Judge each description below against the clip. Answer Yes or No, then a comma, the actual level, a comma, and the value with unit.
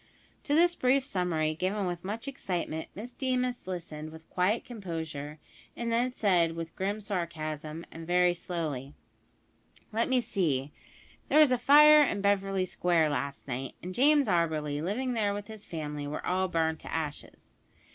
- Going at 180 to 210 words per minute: No, average, 160 wpm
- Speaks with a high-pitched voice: No, medium, 180 Hz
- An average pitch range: No, wide, 6.3 semitones